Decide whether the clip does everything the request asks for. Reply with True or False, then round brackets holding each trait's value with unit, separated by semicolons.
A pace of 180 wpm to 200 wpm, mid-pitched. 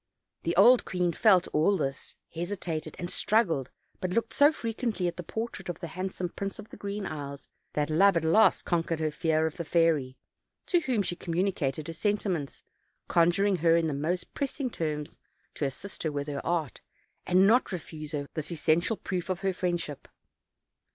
True (185 wpm; 175 Hz)